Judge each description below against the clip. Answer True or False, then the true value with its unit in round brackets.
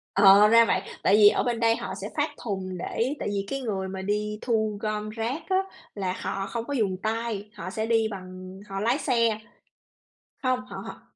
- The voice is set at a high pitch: True (215 Hz)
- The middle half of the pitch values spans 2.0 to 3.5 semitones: True (2.9 semitones)